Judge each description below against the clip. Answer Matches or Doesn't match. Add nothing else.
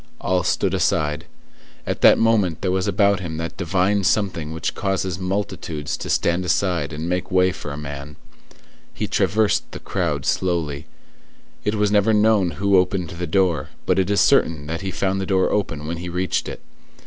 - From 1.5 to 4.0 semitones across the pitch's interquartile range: Matches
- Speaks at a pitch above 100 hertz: Doesn't match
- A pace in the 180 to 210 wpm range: Matches